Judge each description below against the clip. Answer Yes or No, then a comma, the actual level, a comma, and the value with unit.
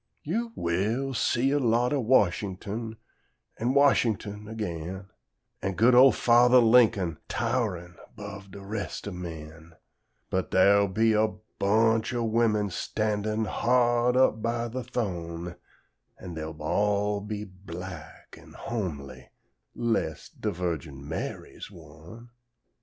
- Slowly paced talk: Yes, slow, 120 wpm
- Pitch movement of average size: Yes, average, 4.7 semitones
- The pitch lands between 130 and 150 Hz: No, low, 105 Hz